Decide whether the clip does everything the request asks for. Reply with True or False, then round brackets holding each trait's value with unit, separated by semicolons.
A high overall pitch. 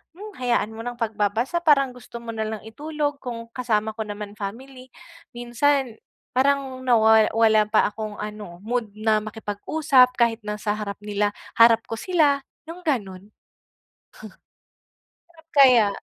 True (230 Hz)